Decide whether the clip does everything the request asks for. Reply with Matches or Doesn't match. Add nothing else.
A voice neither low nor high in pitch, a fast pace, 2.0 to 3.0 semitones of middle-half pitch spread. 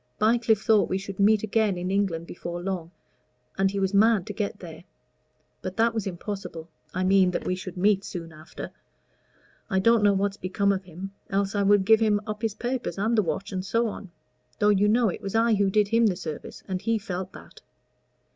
Doesn't match